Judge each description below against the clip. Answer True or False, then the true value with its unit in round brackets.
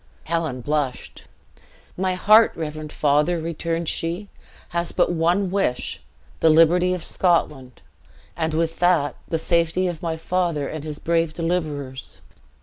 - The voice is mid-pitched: True (165 Hz)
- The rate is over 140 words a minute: False (135 wpm)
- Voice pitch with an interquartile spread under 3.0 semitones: True (2.4 semitones)